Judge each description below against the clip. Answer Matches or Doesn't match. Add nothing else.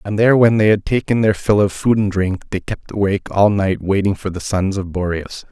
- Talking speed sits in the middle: Doesn't match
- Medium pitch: Doesn't match